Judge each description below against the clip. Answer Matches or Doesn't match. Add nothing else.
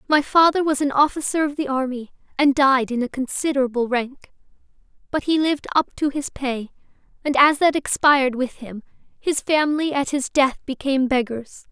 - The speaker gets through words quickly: Doesn't match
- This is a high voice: Matches